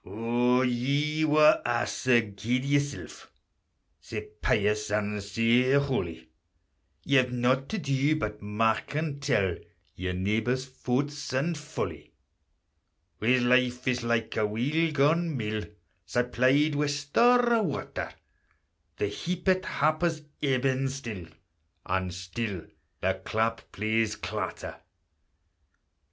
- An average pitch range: Yes, average, 5.0 semitones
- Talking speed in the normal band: No, slow, 115 wpm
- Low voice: Yes, low, 125 Hz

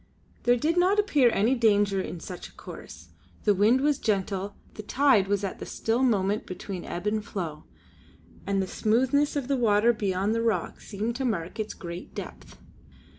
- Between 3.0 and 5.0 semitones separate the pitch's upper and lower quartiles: Yes, average, 4.0 semitones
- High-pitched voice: Yes, high, 215 Hz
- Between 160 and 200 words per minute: Yes, average, 180 wpm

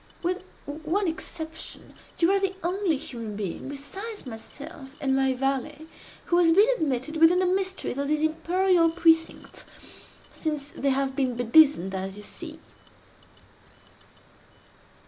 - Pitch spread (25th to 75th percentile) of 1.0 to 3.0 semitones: No, average, 4.4 semitones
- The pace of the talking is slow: Yes, slow, 130 wpm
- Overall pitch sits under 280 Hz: No, very high, 315 Hz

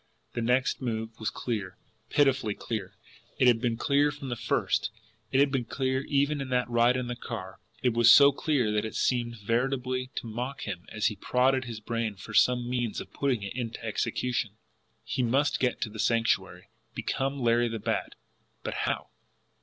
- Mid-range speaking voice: No, low, 120 Hz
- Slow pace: No, average, 185 wpm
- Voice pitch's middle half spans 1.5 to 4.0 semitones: Yes, narrow, 2.6 semitones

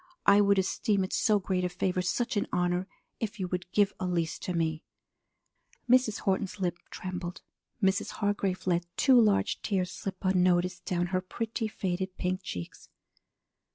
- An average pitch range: No, narrow, 2.2 semitones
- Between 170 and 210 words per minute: No, average, 155 wpm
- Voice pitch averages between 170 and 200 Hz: Yes, medium, 185 Hz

